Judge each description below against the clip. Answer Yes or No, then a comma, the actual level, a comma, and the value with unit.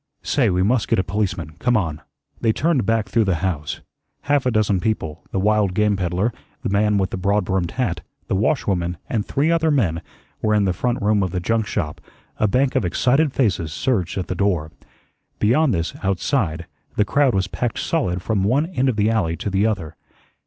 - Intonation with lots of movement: No, average, 4.6 semitones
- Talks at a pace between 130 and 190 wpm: No, fast, 205 wpm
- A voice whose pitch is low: Yes, low, 105 Hz